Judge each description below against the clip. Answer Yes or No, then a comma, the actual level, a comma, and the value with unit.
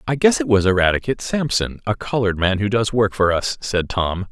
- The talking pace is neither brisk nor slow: No, fast, 220 wpm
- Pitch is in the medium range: No, low, 105 Hz